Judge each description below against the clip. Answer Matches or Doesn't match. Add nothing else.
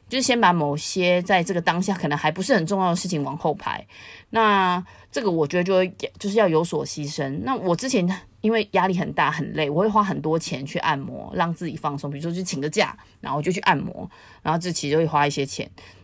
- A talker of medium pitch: Matches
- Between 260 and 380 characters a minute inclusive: Matches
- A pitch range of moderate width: Matches